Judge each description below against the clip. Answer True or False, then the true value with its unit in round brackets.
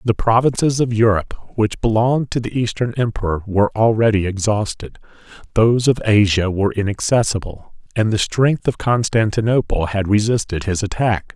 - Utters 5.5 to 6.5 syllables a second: False (5.3 syllables/s)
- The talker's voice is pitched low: True (110 Hz)